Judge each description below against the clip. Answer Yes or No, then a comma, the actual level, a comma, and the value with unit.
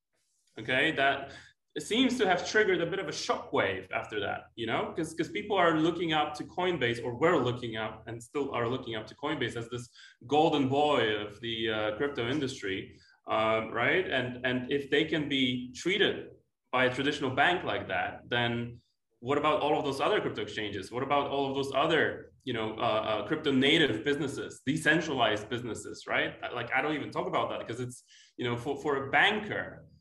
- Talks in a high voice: No, low, 135 Hz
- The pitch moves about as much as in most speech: Yes, average, 4.1 semitones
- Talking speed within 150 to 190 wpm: No, average, 200 wpm